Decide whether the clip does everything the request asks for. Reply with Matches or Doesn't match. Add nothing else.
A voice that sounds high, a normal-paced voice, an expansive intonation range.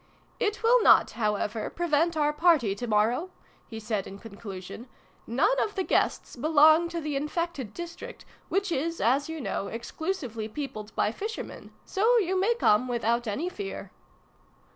Matches